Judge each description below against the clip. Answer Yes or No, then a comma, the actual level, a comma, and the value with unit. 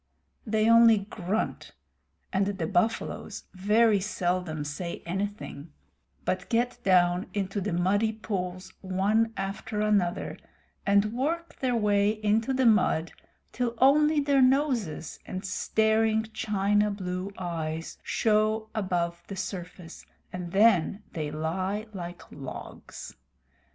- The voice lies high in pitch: Yes, high, 200 Hz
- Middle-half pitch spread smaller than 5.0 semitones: Yes, average, 3.4 semitones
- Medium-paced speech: No, slow, 115 wpm